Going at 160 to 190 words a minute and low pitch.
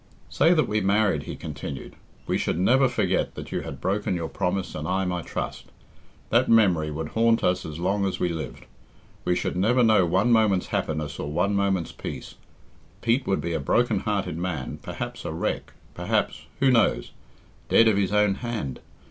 Yes: average, 185 wpm; very low, 95 Hz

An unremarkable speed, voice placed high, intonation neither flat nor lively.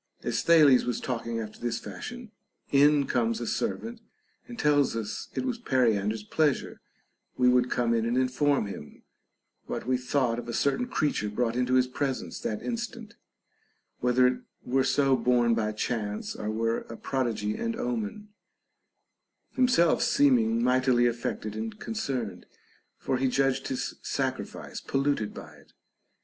No: average, 155 wpm; low, 125 Hz; average, 3.9 semitones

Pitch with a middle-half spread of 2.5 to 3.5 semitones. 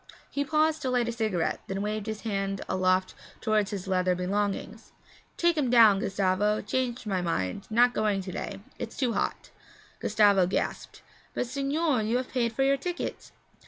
No: average, 4.3 semitones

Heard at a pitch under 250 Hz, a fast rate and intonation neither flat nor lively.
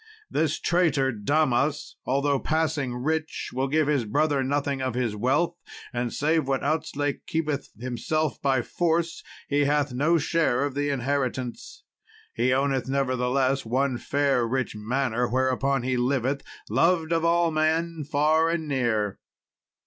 No: medium, 140 Hz; average, 140 wpm; average, 3.4 semitones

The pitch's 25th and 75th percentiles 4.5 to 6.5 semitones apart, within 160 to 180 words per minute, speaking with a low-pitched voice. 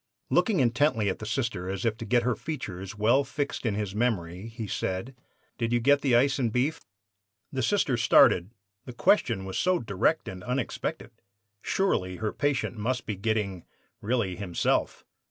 Yes: average, 4.8 semitones; average, 170 wpm; low, 115 Hz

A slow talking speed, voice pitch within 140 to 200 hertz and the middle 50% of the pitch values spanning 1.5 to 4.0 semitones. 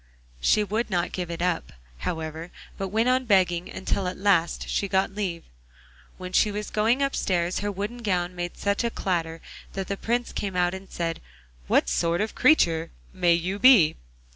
No: average, 185 wpm; high, 190 Hz; average, 3.3 semitones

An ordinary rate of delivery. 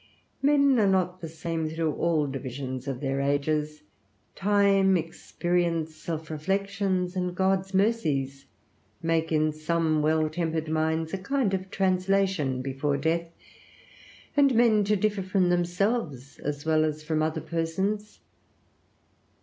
No: slow, 130 wpm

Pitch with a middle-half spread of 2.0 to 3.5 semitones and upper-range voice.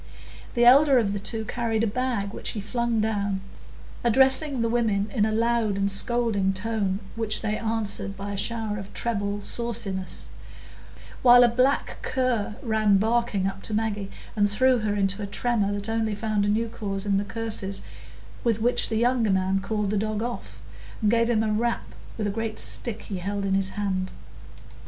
Yes: narrow, 2.6 semitones; high, 215 Hz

